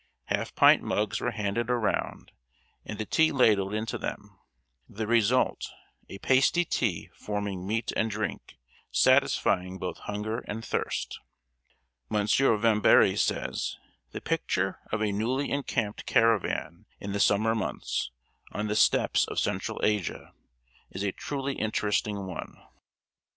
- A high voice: No, low, 105 Hz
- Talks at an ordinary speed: No, slow, 130 wpm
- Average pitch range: No, narrow, 2.2 semitones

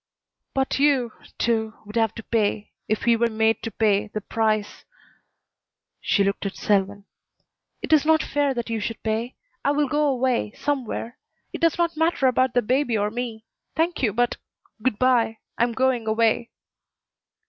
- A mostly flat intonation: No, average, 3.3 semitones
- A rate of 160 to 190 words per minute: Yes, average, 170 wpm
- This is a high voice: Yes, high, 235 Hz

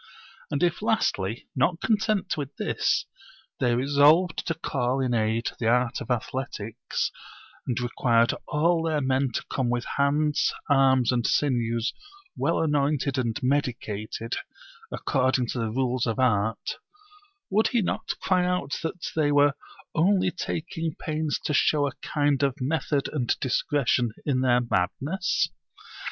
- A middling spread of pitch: Yes, average, 4.1 semitones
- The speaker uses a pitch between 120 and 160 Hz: Yes, low, 135 Hz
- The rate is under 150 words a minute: Yes, average, 140 wpm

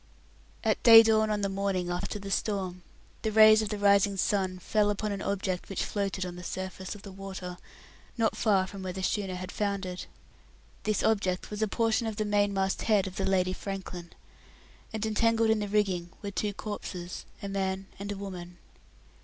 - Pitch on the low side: No, high, 200 Hz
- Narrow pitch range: Yes, narrow, 2.0 semitones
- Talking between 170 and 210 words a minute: Yes, average, 185 wpm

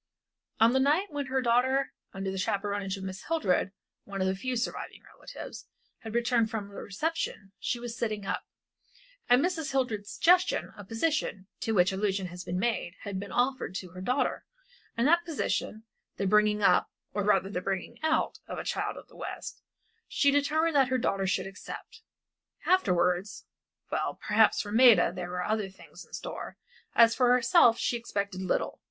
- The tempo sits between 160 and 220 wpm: Yes, average, 180 wpm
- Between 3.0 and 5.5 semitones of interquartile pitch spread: Yes, average, 5.0 semitones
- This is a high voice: Yes, high, 220 Hz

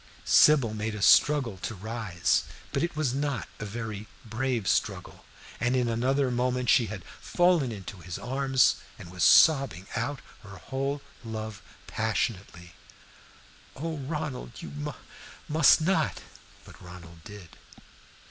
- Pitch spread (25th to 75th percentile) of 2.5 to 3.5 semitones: No, average, 5.0 semitones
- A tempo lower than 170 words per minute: Yes, slow, 135 wpm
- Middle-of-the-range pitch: No, low, 120 Hz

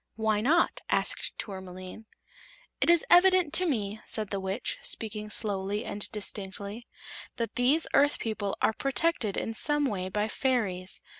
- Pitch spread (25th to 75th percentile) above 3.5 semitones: Yes, wide, 5.4 semitones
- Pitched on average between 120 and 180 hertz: No, high, 220 Hz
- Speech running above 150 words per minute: No, average, 145 wpm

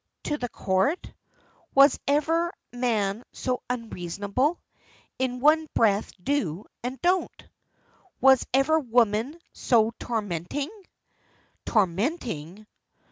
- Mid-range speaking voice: No, high, 245 Hz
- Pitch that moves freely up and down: Yes, wide, 5.8 semitones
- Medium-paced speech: No, slow, 90 wpm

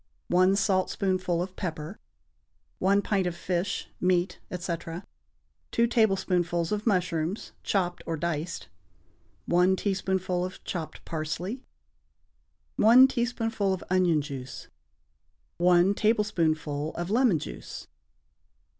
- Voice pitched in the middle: Yes, medium, 180 Hz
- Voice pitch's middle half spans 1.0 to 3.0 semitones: Yes, average, 2.7 semitones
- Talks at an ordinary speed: No, slow, 100 wpm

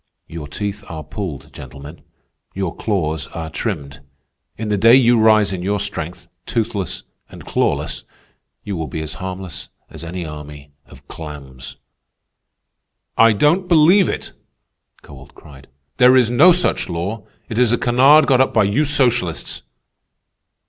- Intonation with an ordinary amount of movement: No, wide, 7.3 semitones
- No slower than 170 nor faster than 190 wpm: No, average, 145 wpm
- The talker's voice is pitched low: Yes, low, 100 Hz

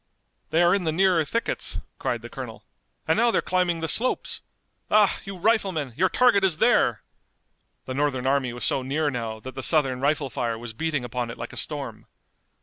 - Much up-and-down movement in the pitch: Yes, wide, 6.3 semitones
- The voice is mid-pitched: Yes, medium, 155 Hz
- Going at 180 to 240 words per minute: Yes, average, 195 wpm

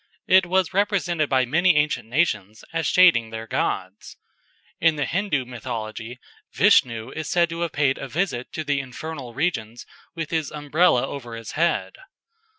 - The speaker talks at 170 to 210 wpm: No, average, 155 wpm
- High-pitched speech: No, medium, 145 Hz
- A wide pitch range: Yes, wide, 5.8 semitones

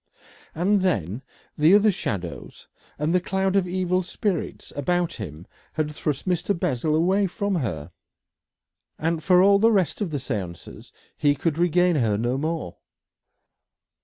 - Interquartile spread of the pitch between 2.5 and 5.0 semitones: No, wide, 5.5 semitones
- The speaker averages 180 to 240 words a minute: No, average, 145 wpm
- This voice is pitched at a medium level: Yes, medium, 165 Hz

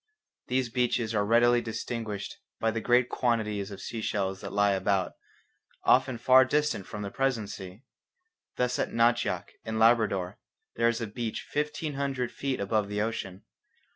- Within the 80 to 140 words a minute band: No, average, 160 wpm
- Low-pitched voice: Yes, low, 115 Hz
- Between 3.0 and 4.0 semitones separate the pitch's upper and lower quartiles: Yes, average, 3.3 semitones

